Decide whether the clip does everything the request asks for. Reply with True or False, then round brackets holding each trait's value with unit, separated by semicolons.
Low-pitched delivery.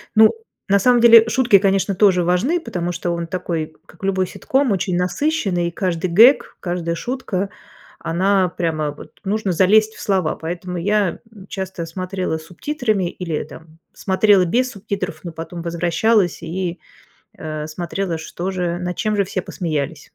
False (185 Hz)